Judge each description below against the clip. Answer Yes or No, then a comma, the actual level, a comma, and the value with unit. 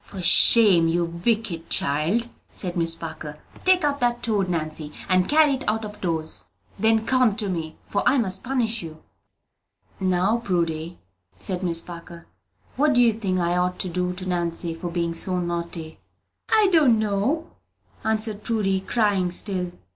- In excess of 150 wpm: Yes, average, 160 wpm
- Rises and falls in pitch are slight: No, average, 4.7 semitones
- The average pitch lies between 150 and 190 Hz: Yes, medium, 185 Hz